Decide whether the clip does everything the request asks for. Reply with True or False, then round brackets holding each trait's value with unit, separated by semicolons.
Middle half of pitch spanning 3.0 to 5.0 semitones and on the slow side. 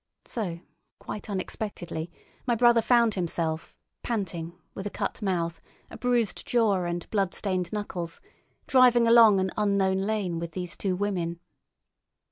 True (4.1 semitones; 130 wpm)